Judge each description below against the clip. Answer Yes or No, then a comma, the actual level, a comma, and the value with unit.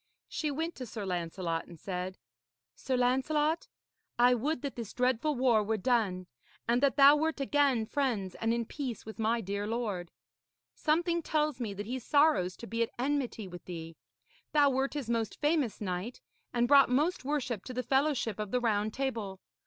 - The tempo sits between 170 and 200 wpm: Yes, average, 180 wpm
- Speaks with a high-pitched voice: Yes, high, 245 Hz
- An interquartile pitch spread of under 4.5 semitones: No, average, 5.1 semitones